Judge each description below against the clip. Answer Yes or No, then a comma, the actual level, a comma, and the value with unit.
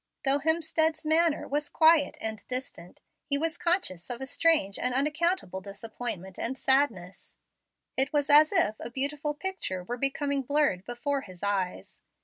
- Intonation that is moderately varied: No, wide, 6.1 semitones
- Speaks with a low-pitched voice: No, very high, 275 Hz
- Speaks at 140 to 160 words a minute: Yes, average, 150 wpm